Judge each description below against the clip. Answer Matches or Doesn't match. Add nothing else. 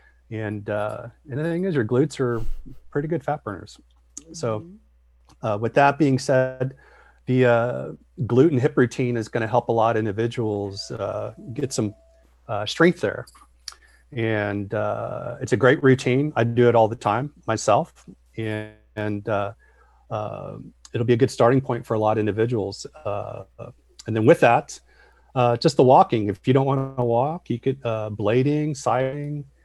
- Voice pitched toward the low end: Matches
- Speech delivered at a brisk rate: Doesn't match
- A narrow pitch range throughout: Doesn't match